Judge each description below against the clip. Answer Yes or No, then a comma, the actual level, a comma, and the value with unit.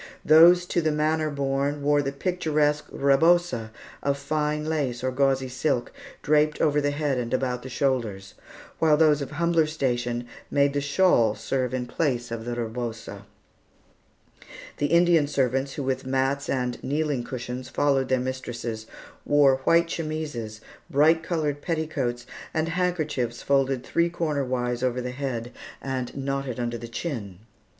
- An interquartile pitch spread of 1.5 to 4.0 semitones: Yes, average, 3.6 semitones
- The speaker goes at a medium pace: Yes, average, 145 wpm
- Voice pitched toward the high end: No, medium, 140 Hz